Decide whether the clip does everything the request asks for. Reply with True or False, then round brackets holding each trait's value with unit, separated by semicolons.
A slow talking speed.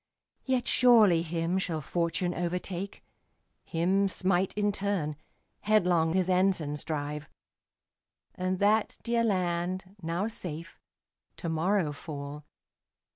True (105 wpm)